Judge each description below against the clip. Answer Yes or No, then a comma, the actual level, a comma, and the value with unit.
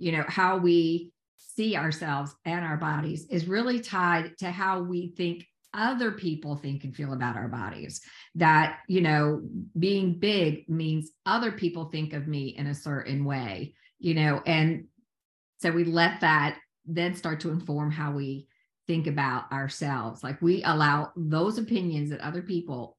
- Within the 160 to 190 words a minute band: Yes, average, 165 wpm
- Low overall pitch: No, medium, 160 Hz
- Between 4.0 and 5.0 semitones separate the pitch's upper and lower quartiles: No, average, 3.4 semitones